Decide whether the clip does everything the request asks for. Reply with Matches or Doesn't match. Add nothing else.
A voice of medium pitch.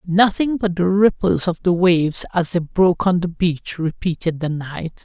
Matches